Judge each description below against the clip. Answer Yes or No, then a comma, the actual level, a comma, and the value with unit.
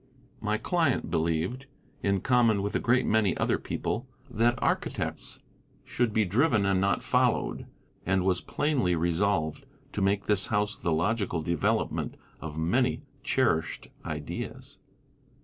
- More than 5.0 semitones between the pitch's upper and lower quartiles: Yes, wide, 5.4 semitones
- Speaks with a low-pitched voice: Yes, low, 100 Hz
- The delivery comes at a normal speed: No, slow, 130 wpm